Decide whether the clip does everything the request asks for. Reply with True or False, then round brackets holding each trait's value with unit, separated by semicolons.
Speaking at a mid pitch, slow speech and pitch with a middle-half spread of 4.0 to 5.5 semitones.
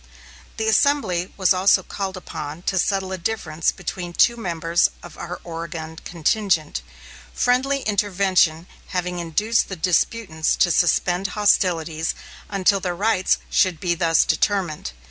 False (180 Hz; 130 wpm; 3.1 semitones)